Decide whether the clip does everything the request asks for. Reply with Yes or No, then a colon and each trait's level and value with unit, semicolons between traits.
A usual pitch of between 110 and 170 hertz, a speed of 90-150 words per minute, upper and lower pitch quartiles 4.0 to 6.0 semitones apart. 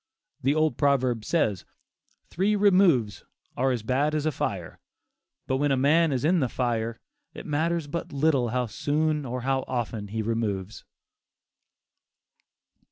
Yes: low, 135 Hz; average, 145 wpm; average, 4.7 semitones